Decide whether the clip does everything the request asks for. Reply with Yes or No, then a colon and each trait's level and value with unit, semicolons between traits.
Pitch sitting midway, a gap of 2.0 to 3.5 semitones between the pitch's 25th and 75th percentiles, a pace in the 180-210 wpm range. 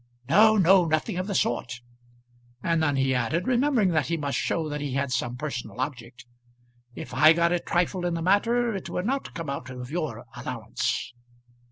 No: medium, 160 Hz; wide, 5.6 semitones; average, 190 wpm